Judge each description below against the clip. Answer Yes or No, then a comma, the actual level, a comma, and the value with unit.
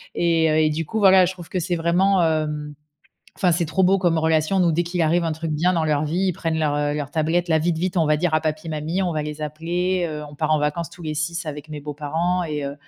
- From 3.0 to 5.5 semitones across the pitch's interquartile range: No, narrow, 2.4 semitones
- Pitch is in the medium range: Yes, medium, 160 Hz